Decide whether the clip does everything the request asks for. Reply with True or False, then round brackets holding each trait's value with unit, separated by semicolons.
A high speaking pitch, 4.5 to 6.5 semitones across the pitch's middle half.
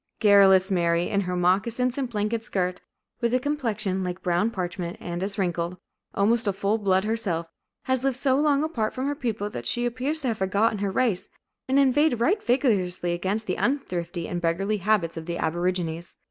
True (200 Hz; 5.2 semitones)